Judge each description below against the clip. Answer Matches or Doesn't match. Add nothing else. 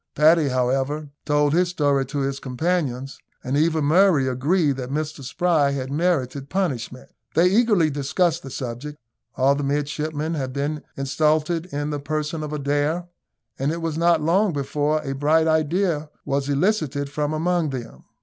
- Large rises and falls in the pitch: Doesn't match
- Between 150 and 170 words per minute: Matches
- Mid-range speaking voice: Matches